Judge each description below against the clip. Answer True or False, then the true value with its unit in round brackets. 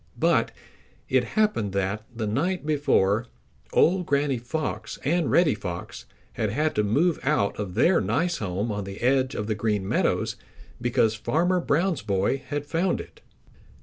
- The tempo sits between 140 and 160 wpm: True (155 wpm)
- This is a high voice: False (125 Hz)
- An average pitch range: False (7.3 semitones)